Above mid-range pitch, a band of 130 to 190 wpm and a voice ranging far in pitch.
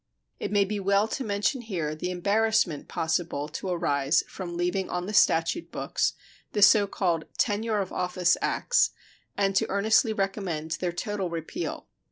No: high, 195 Hz; average, 160 wpm; average, 3.2 semitones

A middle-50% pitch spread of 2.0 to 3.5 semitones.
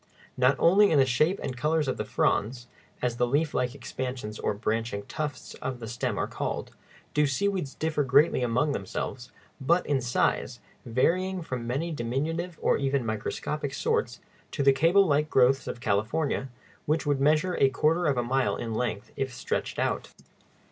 No: average, 4.0 semitones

